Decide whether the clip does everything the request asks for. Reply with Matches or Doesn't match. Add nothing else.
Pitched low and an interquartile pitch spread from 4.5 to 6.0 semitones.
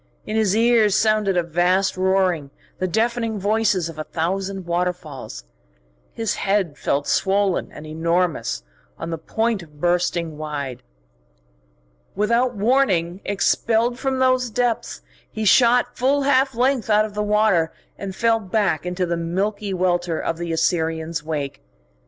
Doesn't match